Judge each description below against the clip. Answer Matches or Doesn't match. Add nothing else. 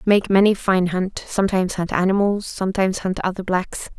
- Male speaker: Doesn't match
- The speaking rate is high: Doesn't match